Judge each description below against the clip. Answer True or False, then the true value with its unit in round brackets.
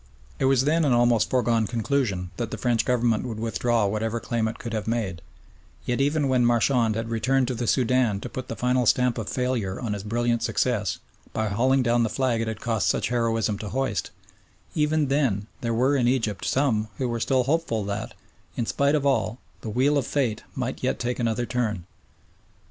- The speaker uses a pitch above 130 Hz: False (120 Hz)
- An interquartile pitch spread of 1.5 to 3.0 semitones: True (2.7 semitones)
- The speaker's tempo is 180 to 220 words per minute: True (200 wpm)